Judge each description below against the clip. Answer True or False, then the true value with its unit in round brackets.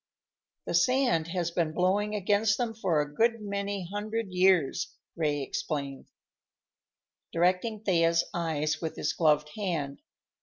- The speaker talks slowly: True (125 wpm)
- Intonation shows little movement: False (4.6 semitones)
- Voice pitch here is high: False (180 Hz)